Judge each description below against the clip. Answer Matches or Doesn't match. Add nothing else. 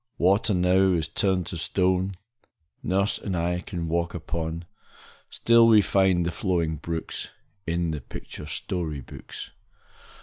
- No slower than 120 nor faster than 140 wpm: Matches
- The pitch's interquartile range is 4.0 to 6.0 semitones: Doesn't match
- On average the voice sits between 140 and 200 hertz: Doesn't match